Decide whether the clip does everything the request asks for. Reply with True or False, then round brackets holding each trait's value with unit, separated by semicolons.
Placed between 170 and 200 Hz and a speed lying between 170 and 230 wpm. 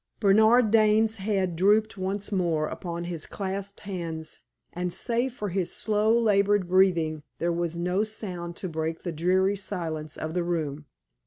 False (185 Hz; 155 wpm)